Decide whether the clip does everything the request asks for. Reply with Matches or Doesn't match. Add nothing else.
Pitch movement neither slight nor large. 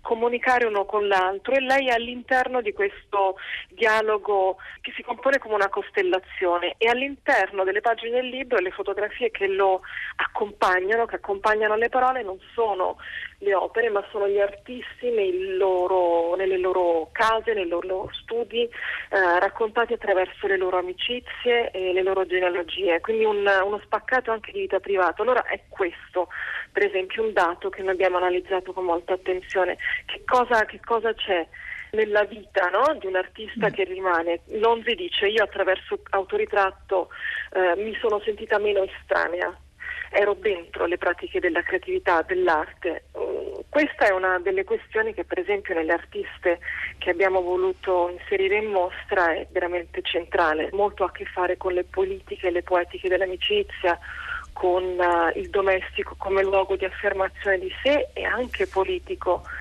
Matches